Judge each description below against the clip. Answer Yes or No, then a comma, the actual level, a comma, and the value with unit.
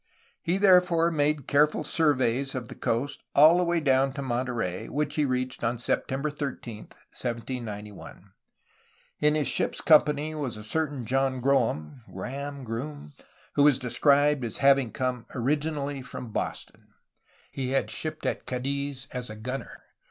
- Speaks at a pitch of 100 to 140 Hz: Yes, low, 135 Hz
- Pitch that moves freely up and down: No, average, 3.2 semitones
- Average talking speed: Yes, average, 145 wpm